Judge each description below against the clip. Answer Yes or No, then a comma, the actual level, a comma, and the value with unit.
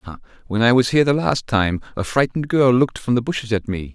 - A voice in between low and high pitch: No, low, 120 Hz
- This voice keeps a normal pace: No, fast, 260 wpm